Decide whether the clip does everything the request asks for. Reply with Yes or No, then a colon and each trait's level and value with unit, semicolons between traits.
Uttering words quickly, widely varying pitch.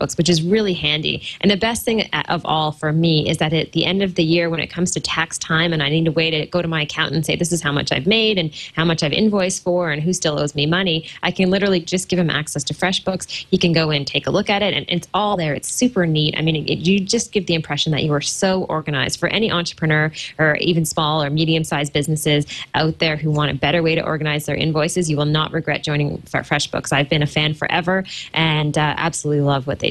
No: fast, 265 wpm; average, 2.8 semitones